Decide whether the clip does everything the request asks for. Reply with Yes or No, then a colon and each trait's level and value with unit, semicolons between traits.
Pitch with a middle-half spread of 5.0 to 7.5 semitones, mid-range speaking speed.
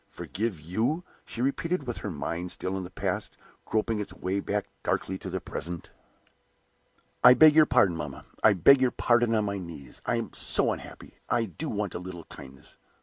Yes: average, 5.3 semitones; average, 195 wpm